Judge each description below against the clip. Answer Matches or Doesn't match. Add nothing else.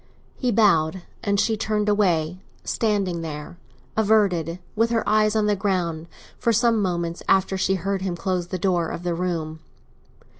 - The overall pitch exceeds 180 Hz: Matches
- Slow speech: Doesn't match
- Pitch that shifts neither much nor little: Matches